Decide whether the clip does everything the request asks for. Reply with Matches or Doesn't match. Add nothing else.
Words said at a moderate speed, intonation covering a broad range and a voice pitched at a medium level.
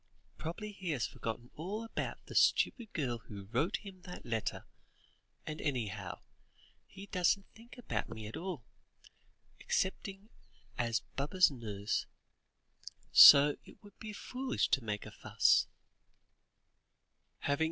Doesn't match